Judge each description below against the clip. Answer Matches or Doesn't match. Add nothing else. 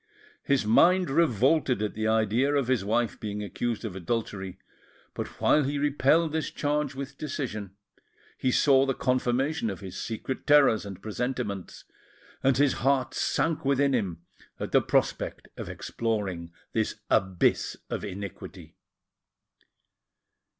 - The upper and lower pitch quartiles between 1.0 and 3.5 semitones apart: Doesn't match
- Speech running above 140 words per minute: Doesn't match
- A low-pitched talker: Matches